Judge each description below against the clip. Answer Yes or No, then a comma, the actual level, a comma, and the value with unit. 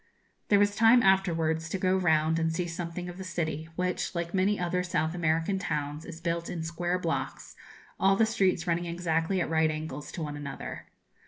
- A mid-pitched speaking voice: Yes, medium, 170 Hz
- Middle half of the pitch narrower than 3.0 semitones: Yes, narrow, 2.4 semitones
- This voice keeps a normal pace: Yes, average, 190 wpm